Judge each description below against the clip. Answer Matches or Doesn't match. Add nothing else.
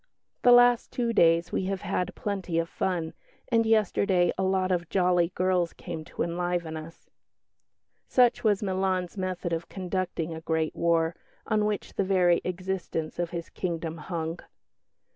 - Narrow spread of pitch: Matches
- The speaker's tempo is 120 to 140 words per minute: Doesn't match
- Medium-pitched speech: Matches